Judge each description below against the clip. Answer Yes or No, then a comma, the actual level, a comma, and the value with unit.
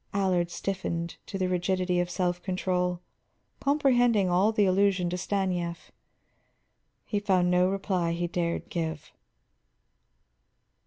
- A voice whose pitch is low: No, medium, 180 Hz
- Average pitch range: No, narrow, 1.9 semitones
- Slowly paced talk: Yes, slow, 115 wpm